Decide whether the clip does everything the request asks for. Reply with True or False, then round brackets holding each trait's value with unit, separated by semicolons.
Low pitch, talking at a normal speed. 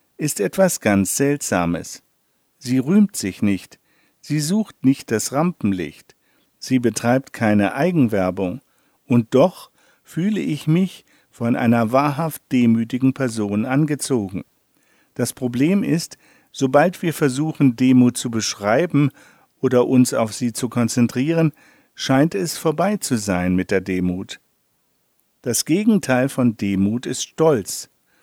False (130 Hz; 120 wpm)